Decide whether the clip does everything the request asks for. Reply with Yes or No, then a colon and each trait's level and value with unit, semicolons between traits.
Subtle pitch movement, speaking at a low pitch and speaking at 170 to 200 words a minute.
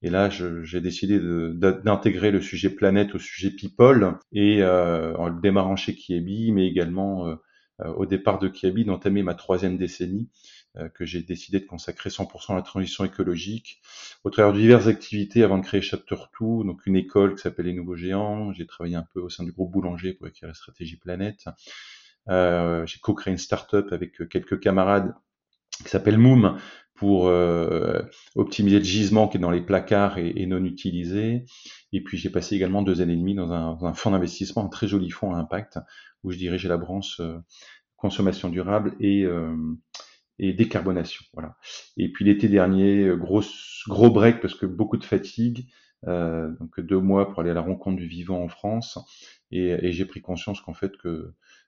Yes: narrow, 2.3 semitones; very low, 95 Hz; average, 195 wpm